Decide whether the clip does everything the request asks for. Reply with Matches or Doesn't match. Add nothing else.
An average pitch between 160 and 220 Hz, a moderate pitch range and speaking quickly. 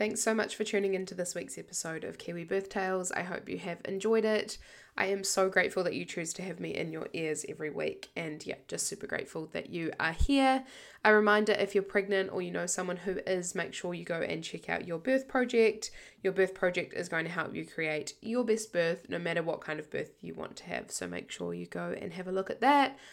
Matches